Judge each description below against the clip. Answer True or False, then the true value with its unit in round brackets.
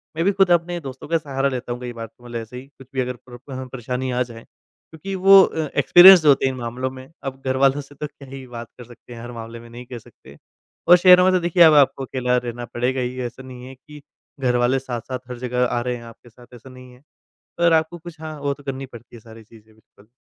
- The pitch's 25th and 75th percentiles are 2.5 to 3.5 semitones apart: True (3.2 semitones)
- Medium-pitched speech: False (130 Hz)